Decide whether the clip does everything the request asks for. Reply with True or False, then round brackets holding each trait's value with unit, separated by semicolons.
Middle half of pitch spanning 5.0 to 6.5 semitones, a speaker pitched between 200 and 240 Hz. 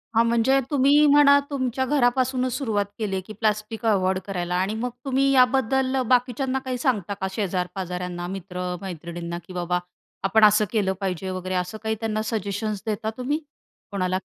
True (5.5 semitones; 215 Hz)